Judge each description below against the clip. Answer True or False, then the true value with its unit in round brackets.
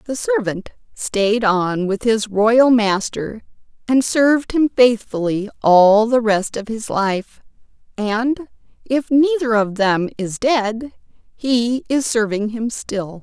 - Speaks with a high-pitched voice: True (225 Hz)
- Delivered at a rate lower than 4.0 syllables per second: True (3.4 syllables/s)